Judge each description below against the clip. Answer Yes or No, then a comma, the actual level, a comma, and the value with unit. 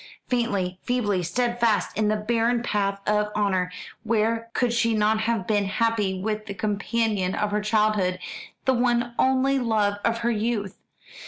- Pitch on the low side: No, high, 215 Hz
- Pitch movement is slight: Yes, narrow, 2.3 semitones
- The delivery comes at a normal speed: Yes, average, 155 wpm